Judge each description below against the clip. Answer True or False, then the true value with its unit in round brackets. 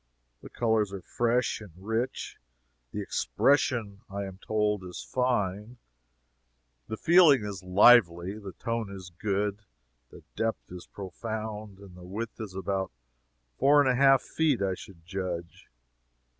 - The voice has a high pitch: False (105 Hz)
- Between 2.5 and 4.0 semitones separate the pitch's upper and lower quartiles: True (3.5 semitones)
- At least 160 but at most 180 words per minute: False (140 wpm)